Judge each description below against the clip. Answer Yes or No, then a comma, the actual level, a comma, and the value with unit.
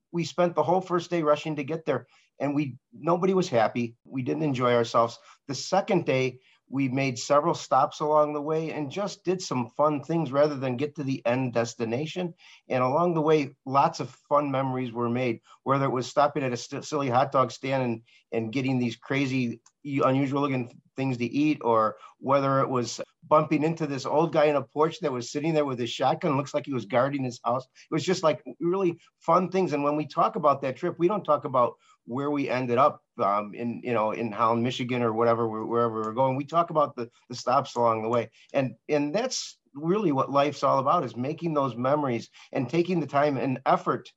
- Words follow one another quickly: Yes, fast, 215 wpm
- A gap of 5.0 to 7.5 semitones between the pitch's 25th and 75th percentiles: No, average, 3.8 semitones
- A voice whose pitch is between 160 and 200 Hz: No, medium, 140 Hz